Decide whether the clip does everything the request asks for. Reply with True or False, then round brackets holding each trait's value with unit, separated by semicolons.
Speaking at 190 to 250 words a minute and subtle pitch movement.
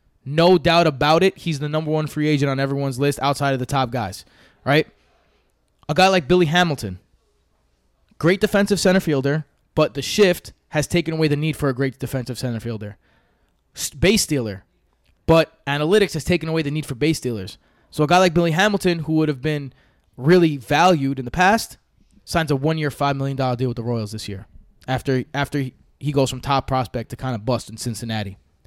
False (195 wpm; 4.3 semitones)